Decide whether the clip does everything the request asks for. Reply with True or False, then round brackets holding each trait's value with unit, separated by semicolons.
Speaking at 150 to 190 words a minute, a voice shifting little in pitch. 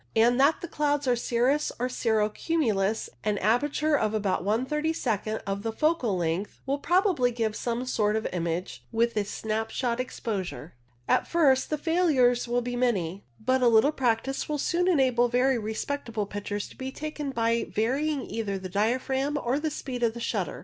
False (180 wpm; 4.4 semitones)